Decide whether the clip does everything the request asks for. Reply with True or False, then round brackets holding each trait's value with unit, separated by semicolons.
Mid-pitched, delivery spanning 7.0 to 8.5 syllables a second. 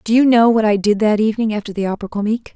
False (215 Hz; 7.8 syllables/s)